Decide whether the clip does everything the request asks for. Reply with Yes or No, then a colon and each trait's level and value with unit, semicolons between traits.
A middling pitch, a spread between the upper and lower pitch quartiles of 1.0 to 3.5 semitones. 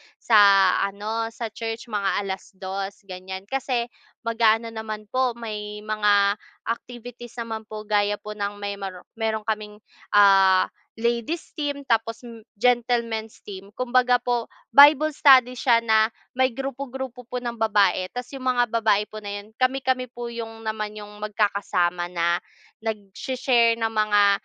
No: high, 220 Hz; average, 2.8 semitones